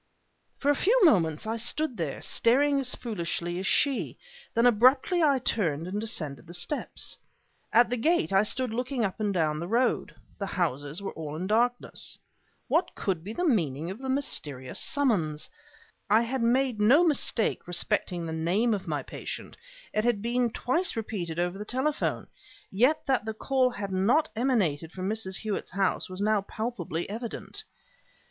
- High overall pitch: Yes, high, 215 Hz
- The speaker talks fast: No, average, 170 wpm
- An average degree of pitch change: No, wide, 6.1 semitones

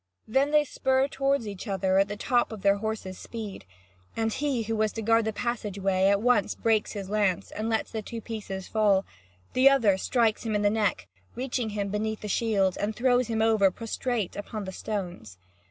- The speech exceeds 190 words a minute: Yes, fast, 205 wpm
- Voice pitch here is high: Yes, high, 215 Hz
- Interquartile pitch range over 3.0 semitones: No, narrow, 2.6 semitones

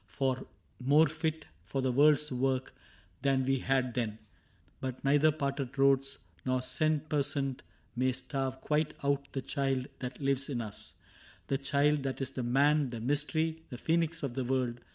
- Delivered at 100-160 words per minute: No, average, 170 wpm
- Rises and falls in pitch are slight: Yes, narrow, 2.2 semitones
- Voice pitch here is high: No, low, 135 Hz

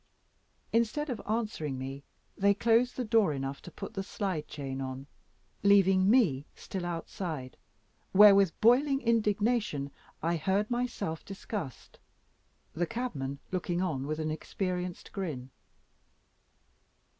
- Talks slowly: Yes, slow, 120 wpm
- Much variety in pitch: Yes, wide, 6.0 semitones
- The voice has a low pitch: No, medium, 185 Hz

